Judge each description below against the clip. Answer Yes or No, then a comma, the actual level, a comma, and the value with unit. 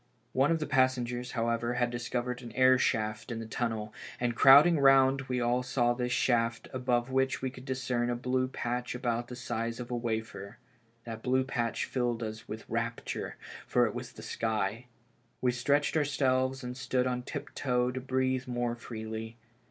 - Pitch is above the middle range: No, low, 125 Hz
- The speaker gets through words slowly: No, average, 175 wpm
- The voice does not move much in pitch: Yes, narrow, 1.7 semitones